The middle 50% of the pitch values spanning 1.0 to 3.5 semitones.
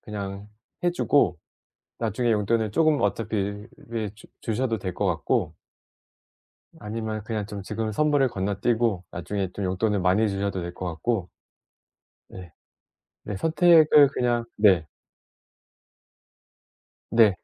Yes: average, 3.1 semitones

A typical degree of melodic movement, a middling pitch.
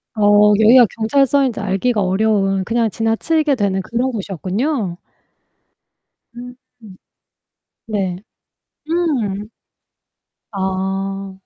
No: average, 4.0 semitones; high, 215 Hz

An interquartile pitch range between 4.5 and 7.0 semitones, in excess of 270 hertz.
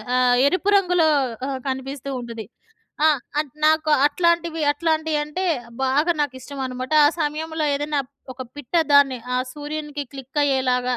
No: average, 3.2 semitones; very high, 290 Hz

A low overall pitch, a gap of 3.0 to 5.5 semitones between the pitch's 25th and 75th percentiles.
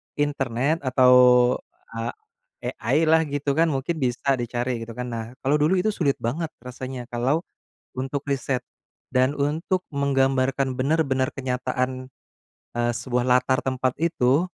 No: low, 130 Hz; narrow, 2.5 semitones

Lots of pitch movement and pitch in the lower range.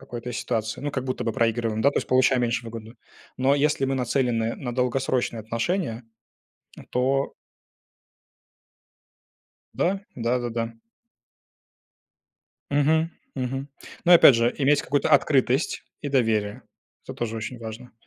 No: average, 2.9 semitones; low, 125 Hz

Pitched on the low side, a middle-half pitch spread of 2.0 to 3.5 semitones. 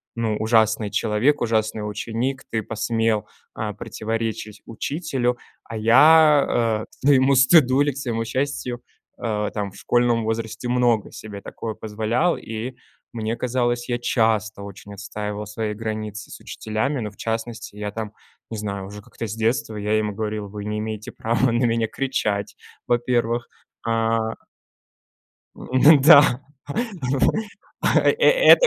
Yes: low, 115 Hz; average, 2.7 semitones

